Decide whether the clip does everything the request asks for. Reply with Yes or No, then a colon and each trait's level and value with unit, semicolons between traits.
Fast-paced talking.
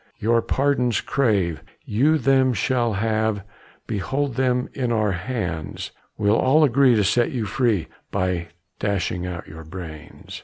No: average, 140 wpm